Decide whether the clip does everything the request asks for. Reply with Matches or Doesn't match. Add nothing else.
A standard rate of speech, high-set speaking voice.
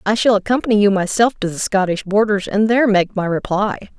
Doesn't match